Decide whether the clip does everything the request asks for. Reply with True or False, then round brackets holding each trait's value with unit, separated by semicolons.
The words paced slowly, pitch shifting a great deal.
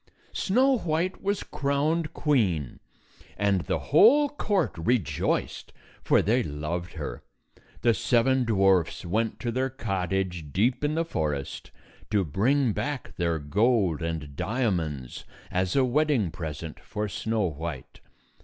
True (125 wpm; 8.6 semitones)